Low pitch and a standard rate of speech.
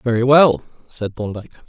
Yes: low, 120 Hz; average, 145 wpm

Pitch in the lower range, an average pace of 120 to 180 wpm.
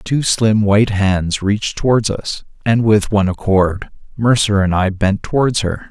Yes: low, 105 Hz; average, 175 wpm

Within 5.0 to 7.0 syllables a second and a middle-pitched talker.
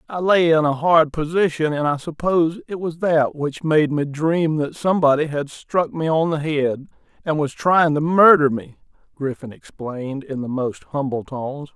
No: 4.7 syllables/s; medium, 150 Hz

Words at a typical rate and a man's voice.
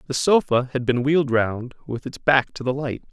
No: fast, 230 wpm; male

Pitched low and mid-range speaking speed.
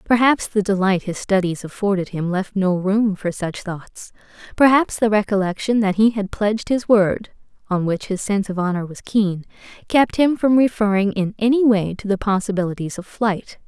No: high, 205 Hz; average, 185 wpm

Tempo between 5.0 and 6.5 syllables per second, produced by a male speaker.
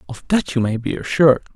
Yes: 6.3 syllables/s; male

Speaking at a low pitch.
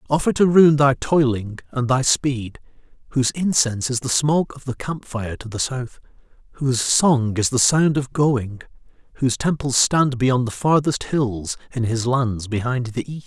Yes: low, 130 Hz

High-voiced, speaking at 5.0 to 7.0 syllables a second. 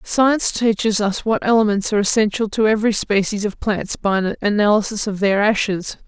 Yes: high, 210 Hz; 5.5 syllables/s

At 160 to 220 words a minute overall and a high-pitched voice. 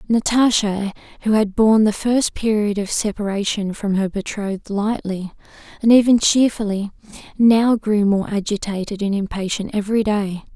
No: slow, 135 wpm; high, 210 Hz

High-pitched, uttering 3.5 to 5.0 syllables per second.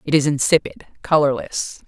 No: medium, 145 Hz; 4.9 syllables/s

